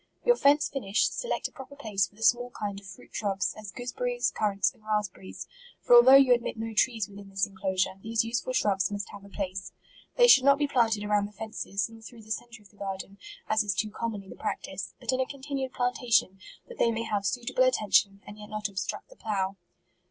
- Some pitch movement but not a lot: Yes, average, 3.7 semitones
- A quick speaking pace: Yes, fast, 235 wpm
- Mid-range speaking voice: No, high, 215 Hz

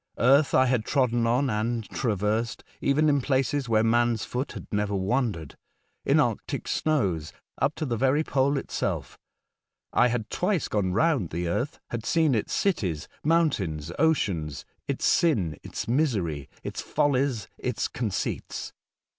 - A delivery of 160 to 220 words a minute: No, average, 145 wpm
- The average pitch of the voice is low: Yes, low, 120 Hz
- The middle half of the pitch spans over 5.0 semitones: Yes, wide, 5.5 semitones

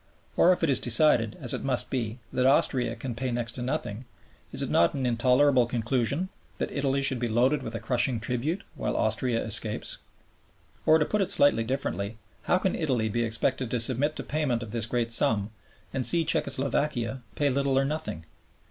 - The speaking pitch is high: No, low, 125 Hz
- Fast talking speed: No, average, 195 wpm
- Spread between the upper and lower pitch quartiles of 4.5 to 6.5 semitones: No, average, 3.3 semitones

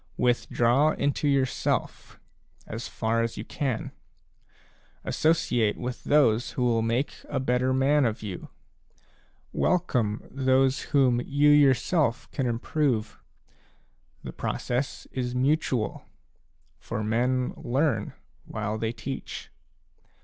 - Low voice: Yes, low, 125 Hz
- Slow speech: Yes, slow, 110 wpm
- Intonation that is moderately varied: Yes, average, 3.3 semitones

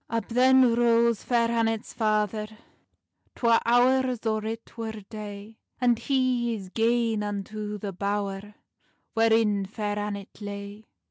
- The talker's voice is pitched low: No, high, 220 Hz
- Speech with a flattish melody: Yes, narrow, 2.2 semitones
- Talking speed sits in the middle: No, slow, 125 wpm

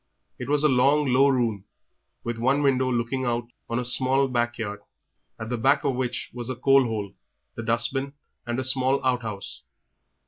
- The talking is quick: No, average, 180 wpm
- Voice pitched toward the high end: No, low, 125 Hz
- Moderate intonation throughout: No, narrow, 2.2 semitones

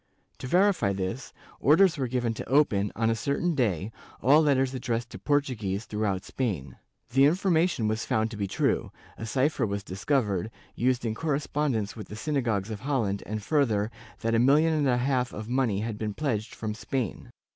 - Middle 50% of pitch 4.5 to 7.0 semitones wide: Yes, average, 4.8 semitones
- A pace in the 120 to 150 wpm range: No, average, 180 wpm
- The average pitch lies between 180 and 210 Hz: No, low, 120 Hz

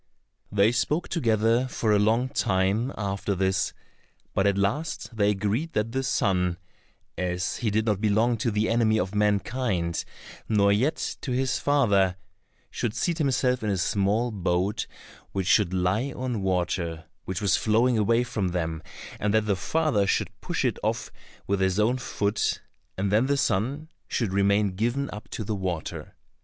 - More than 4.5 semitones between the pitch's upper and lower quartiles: No, average, 3.7 semitones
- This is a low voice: Yes, low, 105 Hz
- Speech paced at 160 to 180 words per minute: Yes, average, 165 wpm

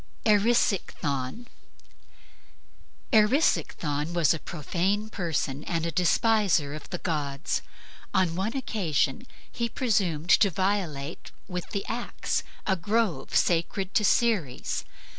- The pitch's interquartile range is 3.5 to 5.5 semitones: Yes, average, 5.2 semitones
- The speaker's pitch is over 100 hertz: Yes, medium, 185 Hz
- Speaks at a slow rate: Yes, slow, 105 wpm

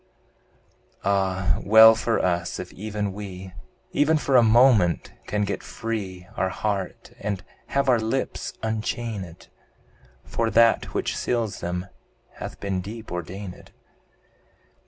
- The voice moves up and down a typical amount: Yes, average, 3.4 semitones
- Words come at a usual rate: No, slow, 120 wpm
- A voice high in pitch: No, low, 105 Hz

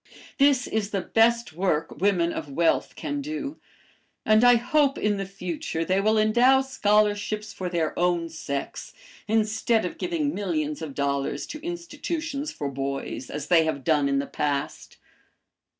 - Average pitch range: No, wide, 7.5 semitones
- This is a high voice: Yes, high, 200 Hz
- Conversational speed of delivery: Yes, average, 155 wpm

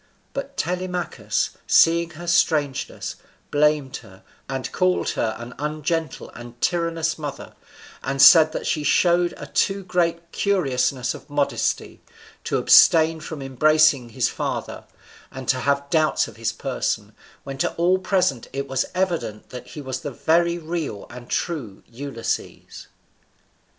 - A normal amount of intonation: Yes, average, 4.2 semitones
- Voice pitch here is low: No, medium, 155 Hz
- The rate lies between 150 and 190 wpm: No, average, 140 wpm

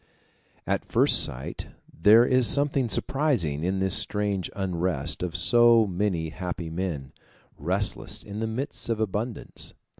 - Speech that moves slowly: Yes, slow, 130 wpm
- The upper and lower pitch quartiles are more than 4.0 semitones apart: Yes, average, 4.7 semitones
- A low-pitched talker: Yes, low, 100 Hz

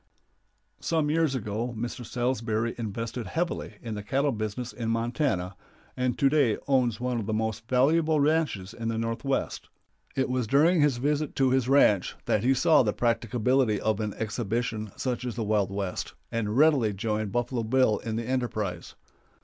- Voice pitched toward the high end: No, low, 120 Hz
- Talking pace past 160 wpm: Yes, average, 170 wpm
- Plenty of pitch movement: No, average, 3.4 semitones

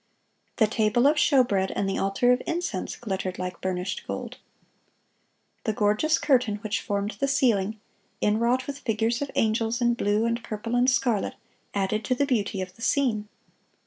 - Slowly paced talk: No, average, 165 wpm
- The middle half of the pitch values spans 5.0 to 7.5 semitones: No, average, 3.4 semitones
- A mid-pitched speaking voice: No, high, 225 Hz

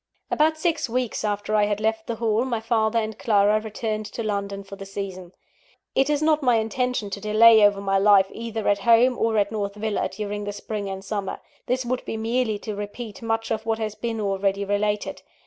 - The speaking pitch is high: Yes, high, 215 Hz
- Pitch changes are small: Yes, narrow, 2.1 semitones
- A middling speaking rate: No, fast, 210 wpm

